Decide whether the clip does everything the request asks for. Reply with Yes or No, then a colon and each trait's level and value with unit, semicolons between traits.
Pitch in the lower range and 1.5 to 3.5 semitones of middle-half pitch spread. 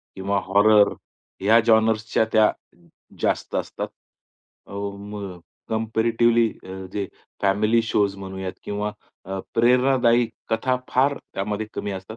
Yes: low, 105 Hz; narrow, 2.4 semitones